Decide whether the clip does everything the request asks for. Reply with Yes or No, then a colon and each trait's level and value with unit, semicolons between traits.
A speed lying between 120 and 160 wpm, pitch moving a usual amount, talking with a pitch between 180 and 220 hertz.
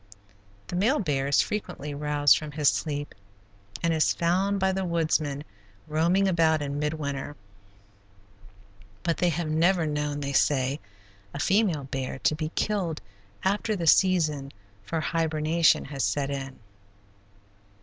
No: average, 140 wpm; average, 3.2 semitones; medium, 155 Hz